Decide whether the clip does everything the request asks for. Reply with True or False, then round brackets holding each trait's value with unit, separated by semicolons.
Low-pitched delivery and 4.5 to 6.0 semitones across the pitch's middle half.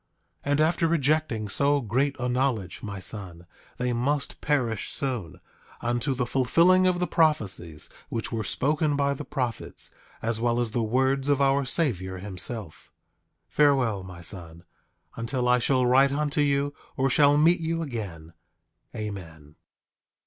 True (125 Hz; 5.1 semitones)